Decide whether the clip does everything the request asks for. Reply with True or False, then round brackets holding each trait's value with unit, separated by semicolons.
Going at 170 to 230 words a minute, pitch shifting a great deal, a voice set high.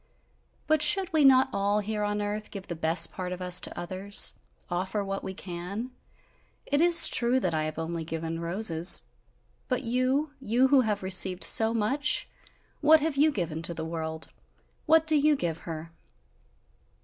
True (175 wpm; 7.5 semitones; 205 Hz)